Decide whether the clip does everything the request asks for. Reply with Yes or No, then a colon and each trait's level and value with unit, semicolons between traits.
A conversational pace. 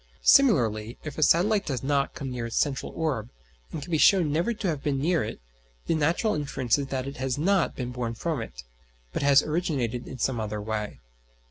No: fast, 210 wpm